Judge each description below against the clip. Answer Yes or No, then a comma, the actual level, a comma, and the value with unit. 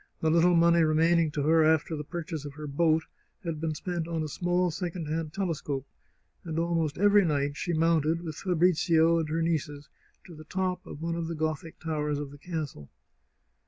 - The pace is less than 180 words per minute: No, average, 195 wpm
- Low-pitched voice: No, medium, 160 Hz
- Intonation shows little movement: Yes, narrow, 1.8 semitones